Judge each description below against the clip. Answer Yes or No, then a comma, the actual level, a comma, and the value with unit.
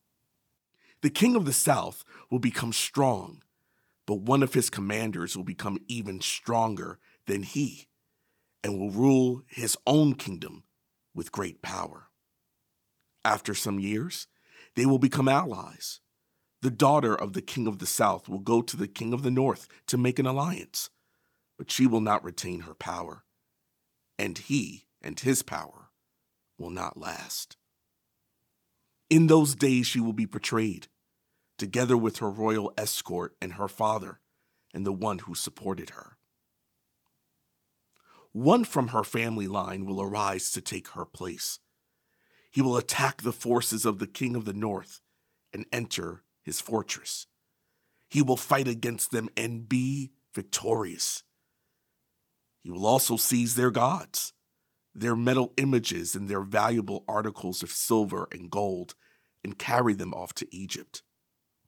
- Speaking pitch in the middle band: No, low, 115 Hz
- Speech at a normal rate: Yes, average, 145 wpm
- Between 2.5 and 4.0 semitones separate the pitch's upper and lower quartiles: No, average, 4.4 semitones